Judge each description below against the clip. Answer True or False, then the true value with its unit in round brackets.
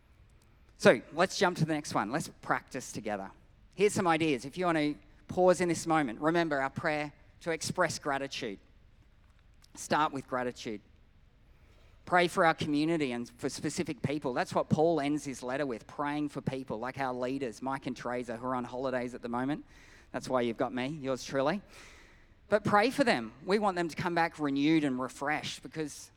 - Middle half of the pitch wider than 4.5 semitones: True (5.1 semitones)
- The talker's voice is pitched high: False (140 Hz)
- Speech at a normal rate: True (190 wpm)